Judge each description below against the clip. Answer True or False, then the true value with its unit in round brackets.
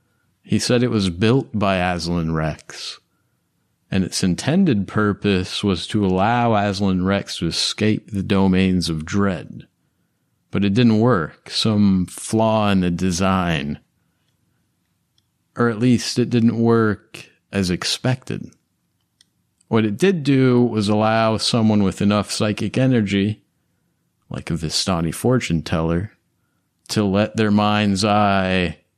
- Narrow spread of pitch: False (3.2 semitones)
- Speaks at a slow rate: True (125 wpm)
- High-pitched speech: False (100 Hz)